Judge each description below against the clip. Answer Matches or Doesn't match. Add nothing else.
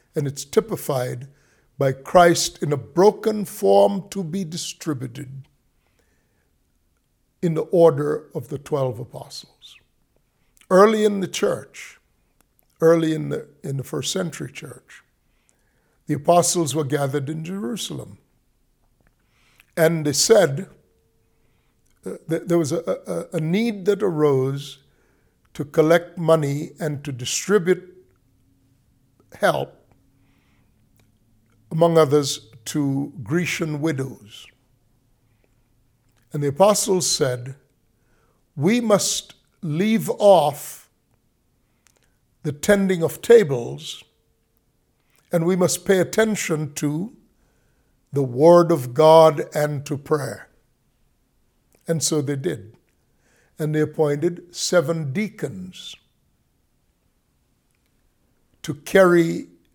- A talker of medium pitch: Matches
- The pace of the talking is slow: Matches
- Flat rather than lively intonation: Doesn't match